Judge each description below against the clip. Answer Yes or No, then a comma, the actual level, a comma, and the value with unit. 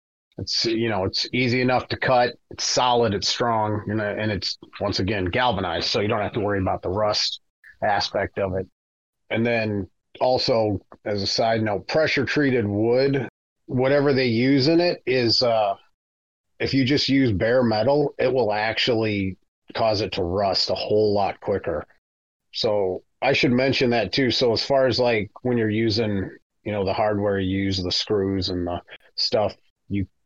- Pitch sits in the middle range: No, low, 110 Hz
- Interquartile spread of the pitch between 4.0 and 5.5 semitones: Yes, average, 4.4 semitones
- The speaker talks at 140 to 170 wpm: No, average, 180 wpm